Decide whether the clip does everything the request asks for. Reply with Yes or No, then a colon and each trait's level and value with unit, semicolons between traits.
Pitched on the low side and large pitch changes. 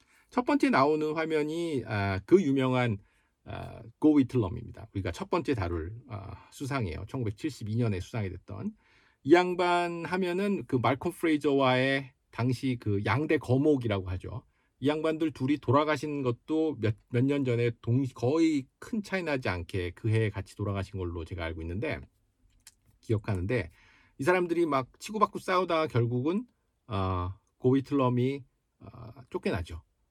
Yes: low, 125 Hz; wide, 6.9 semitones